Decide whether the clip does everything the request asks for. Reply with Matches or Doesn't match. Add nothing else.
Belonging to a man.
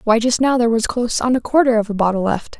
Doesn't match